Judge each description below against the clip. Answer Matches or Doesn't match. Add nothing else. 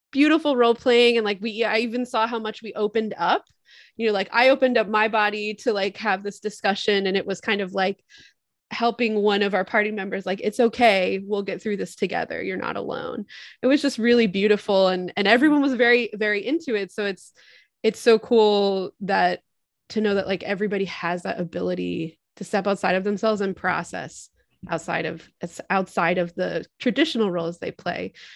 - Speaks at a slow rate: Doesn't match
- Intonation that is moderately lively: Matches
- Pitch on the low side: Doesn't match